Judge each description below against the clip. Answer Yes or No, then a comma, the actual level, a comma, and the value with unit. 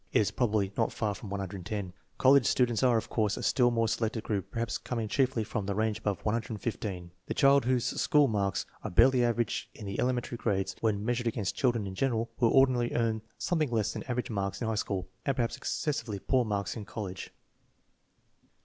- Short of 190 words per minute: No, average, 200 wpm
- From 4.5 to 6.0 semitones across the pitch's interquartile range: No, average, 3.2 semitones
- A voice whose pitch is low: Yes, low, 110 Hz